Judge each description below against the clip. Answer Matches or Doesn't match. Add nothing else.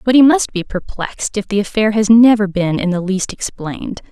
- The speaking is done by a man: Doesn't match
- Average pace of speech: Doesn't match